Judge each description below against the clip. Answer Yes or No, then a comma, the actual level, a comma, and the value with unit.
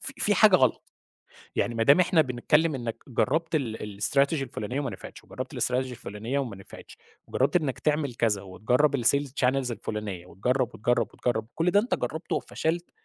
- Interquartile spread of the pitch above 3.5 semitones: Yes, average, 4.6 semitones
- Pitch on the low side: Yes, low, 125 Hz